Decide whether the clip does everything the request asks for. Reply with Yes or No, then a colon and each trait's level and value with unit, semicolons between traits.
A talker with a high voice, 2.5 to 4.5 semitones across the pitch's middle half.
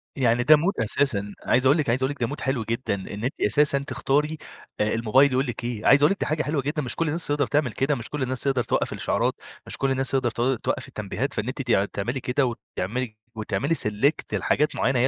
No: low, 130 Hz; average, 3.5 semitones